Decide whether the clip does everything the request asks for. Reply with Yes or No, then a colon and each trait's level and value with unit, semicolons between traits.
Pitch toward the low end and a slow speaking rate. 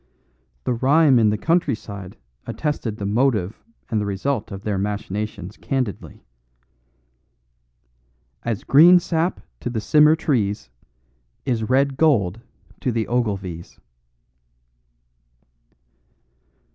Yes: low, 115 Hz; slow, 105 wpm